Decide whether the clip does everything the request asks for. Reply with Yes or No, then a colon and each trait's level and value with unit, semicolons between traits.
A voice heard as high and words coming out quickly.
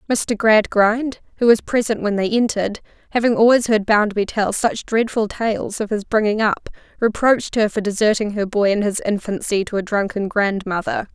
No: high, 215 Hz; average, 180 wpm